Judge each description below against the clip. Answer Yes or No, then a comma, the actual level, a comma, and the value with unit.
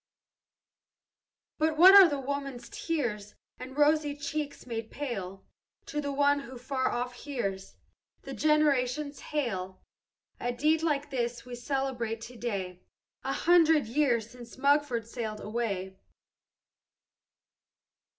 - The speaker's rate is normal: No, slow, 110 wpm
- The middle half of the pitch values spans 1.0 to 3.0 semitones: No, average, 4.0 semitones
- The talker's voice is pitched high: Yes, very high, 260 Hz